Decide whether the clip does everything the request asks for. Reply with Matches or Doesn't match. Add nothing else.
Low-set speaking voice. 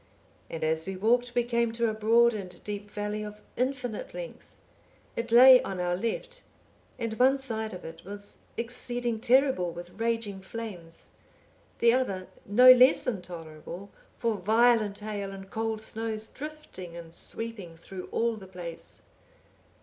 Doesn't match